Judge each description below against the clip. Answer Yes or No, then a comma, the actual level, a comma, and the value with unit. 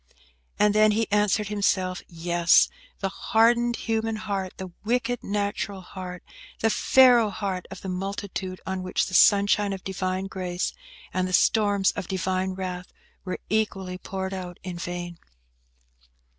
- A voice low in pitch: No, high, 195 Hz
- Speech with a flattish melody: Yes, narrow, 2.2 semitones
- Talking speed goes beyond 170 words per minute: No, average, 140 wpm